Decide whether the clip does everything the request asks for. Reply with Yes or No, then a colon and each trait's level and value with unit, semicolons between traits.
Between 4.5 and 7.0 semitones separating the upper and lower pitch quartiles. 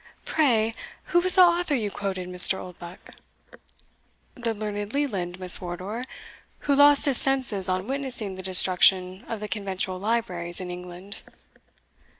Yes: wide, 5.4 semitones